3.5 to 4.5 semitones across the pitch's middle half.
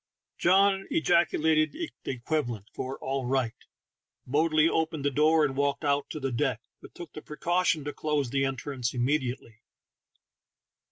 No: average, 3.1 semitones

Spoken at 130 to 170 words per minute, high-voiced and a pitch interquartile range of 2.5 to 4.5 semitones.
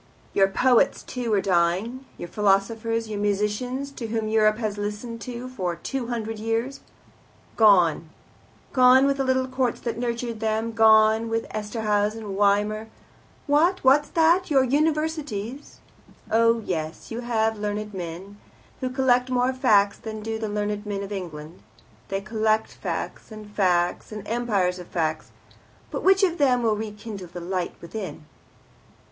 Yes: average, 150 wpm; high, 220 Hz; average, 3.4 semitones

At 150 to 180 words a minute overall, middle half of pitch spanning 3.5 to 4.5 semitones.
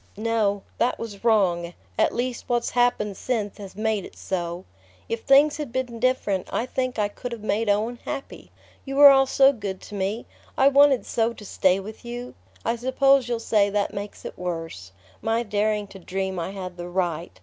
No: average, 195 wpm; average, 4.0 semitones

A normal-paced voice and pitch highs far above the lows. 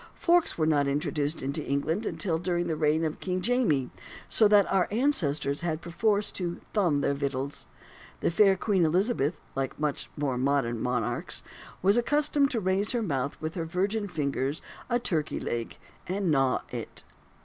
Yes: average, 170 wpm; wide, 6.1 semitones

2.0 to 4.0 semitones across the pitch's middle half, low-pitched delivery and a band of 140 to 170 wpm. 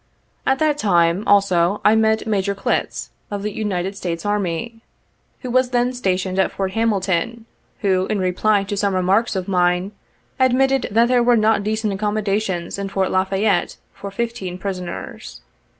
No: average, 2.9 semitones; high, 200 Hz; average, 160 wpm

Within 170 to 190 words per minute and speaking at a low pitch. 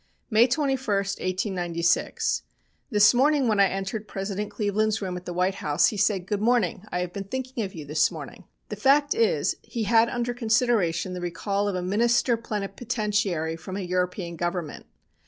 No: average, 175 wpm; high, 200 Hz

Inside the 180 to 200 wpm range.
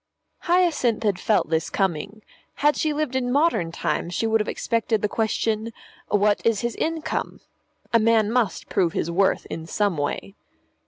No: average, 165 wpm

